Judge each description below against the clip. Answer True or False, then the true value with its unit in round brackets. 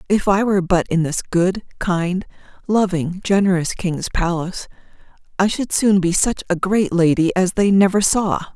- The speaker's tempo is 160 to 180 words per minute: True (170 wpm)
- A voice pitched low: False (185 Hz)